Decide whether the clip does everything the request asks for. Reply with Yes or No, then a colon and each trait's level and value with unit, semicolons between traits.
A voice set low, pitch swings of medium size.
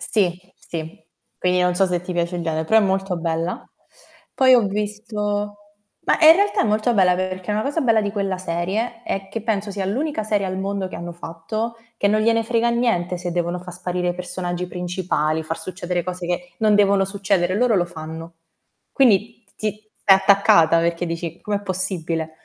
No: high, 190 Hz; average, 3.3 semitones